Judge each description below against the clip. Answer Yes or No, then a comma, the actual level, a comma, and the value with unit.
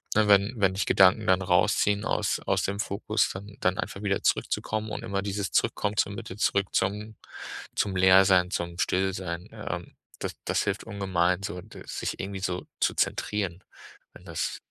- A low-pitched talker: Yes, very low, 95 Hz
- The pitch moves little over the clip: Yes, narrow, 1.7 semitones